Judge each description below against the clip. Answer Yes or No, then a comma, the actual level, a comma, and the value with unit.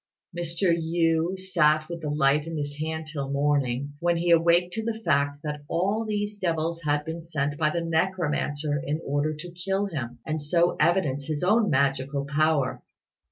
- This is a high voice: No, medium, 160 Hz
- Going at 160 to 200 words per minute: Yes, average, 175 wpm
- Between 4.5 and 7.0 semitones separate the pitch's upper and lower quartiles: No, average, 3.0 semitones